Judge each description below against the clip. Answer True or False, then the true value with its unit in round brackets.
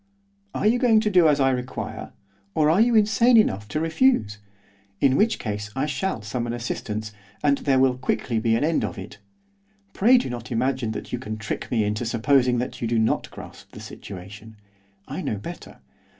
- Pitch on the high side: False (130 Hz)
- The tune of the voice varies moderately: False (6.5 semitones)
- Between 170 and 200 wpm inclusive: True (195 wpm)